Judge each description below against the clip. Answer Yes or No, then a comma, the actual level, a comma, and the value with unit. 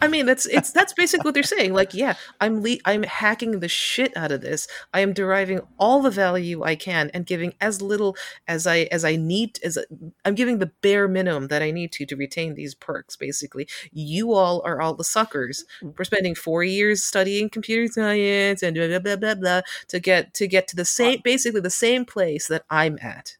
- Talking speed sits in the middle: No, fast, 220 wpm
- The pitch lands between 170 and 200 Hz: Yes, high, 190 Hz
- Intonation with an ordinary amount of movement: Yes, average, 4.3 semitones